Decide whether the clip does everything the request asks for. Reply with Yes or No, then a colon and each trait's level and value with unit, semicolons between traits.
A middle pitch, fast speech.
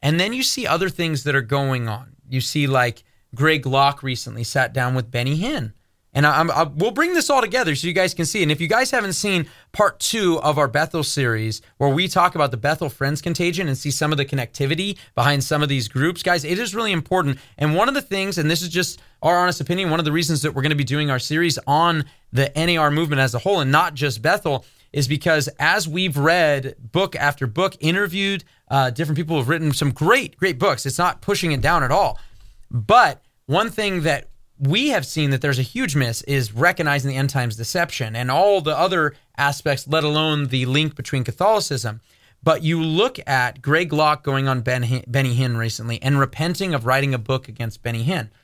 Yes: medium, 145 Hz; fast, 225 wpm